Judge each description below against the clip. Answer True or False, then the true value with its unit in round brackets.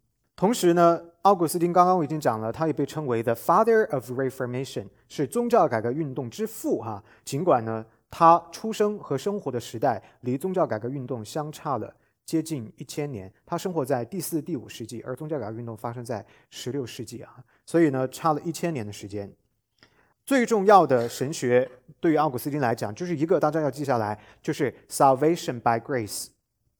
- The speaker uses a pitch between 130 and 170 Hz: True (140 Hz)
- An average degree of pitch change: False (5.9 semitones)